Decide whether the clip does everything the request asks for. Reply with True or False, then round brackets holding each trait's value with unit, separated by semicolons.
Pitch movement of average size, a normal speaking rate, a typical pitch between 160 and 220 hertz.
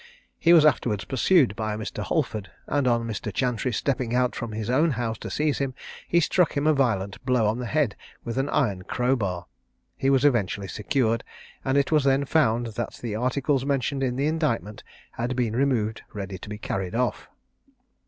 False (4.1 semitones; 190 wpm; 125 Hz)